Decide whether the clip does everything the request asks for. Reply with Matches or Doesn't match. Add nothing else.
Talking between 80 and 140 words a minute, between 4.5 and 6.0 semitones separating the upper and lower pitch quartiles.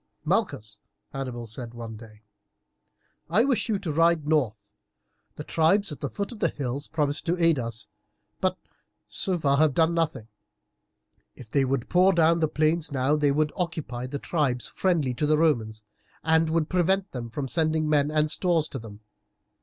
Doesn't match